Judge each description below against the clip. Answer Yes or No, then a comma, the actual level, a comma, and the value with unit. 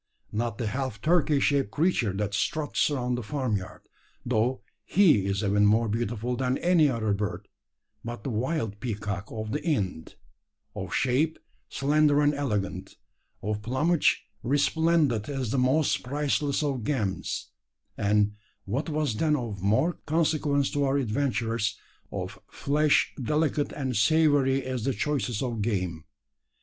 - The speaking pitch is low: Yes, low, 125 Hz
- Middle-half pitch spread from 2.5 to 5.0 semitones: No, wide, 5.5 semitones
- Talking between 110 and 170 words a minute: Yes, average, 140 wpm